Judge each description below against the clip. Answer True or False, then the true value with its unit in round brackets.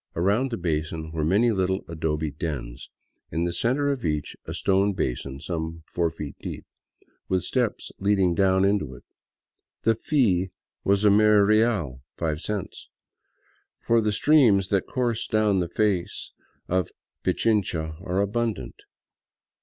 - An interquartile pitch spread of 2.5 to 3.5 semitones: False (4.7 semitones)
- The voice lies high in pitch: False (95 Hz)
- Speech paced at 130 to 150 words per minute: True (140 wpm)